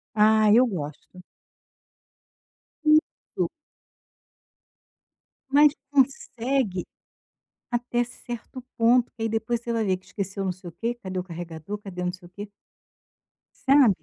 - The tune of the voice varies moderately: Yes, average, 4.6 semitones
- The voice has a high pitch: Yes, high, 220 Hz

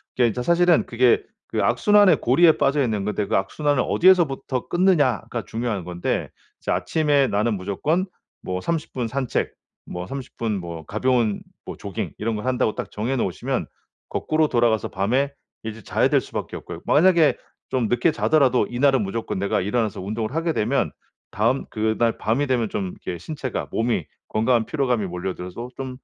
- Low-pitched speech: Yes, low, 120 Hz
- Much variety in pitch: No, average, 4.8 semitones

